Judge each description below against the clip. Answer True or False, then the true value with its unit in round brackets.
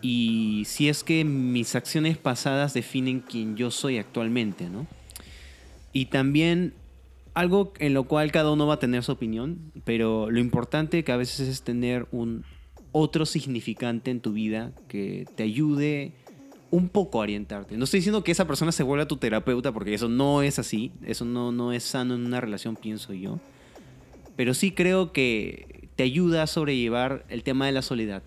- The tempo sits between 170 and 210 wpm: True (180 wpm)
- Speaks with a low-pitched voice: True (125 Hz)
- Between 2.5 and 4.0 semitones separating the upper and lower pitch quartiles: False (4.8 semitones)